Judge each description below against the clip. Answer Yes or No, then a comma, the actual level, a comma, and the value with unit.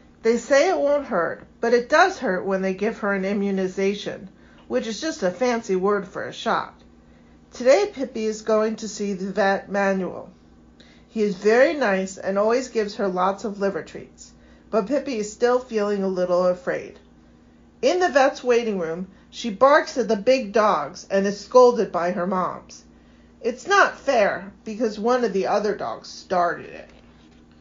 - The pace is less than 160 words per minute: No, average, 175 wpm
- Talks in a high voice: Yes, high, 205 Hz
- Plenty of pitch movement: No, average, 4.3 semitones